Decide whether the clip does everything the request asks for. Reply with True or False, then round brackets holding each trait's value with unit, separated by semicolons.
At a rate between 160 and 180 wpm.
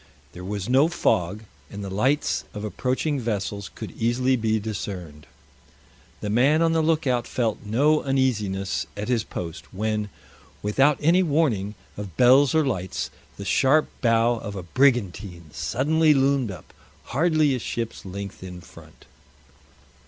False (145 wpm)